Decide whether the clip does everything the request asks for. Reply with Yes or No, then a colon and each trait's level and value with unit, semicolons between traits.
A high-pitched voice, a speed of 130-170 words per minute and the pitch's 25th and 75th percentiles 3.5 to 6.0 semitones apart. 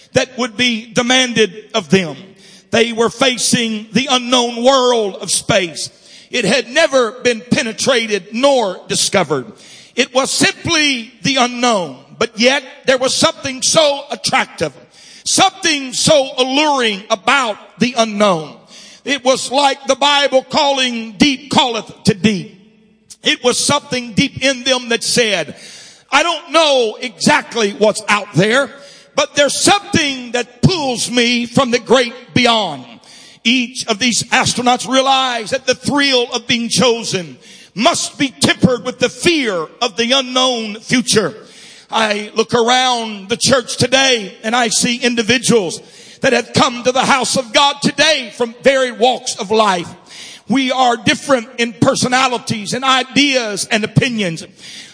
No: high, 245 Hz; average, 140 wpm; average, 3.0 semitones